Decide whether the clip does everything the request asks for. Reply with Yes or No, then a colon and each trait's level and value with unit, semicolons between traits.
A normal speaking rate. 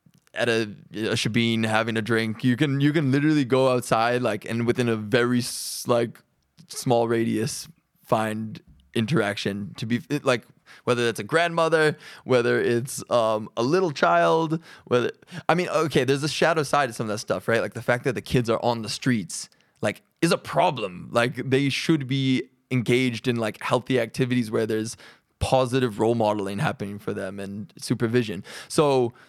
Yes: average, 175 wpm